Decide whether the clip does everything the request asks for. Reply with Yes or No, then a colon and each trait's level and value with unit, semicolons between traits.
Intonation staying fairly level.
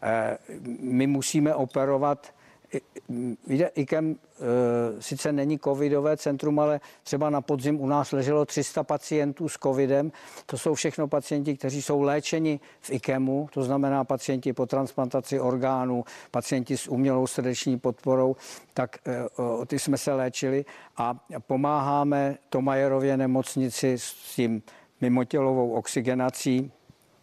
Yes: narrow, 2.0 semitones